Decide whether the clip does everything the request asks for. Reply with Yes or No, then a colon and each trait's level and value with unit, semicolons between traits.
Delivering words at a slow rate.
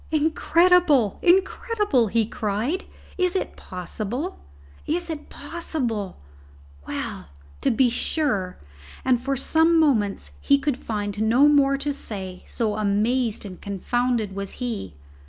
Yes: slow, 120 wpm